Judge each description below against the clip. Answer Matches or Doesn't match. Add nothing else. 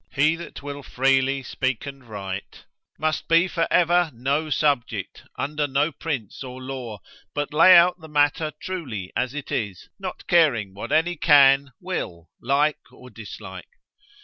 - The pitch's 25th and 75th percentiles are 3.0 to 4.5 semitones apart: Matches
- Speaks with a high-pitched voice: Doesn't match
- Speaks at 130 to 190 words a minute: Matches